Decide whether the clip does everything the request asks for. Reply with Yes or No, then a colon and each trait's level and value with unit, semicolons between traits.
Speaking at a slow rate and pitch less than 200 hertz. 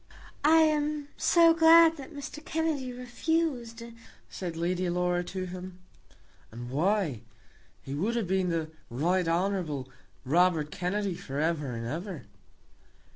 Yes: slow, 130 wpm; medium, 185 Hz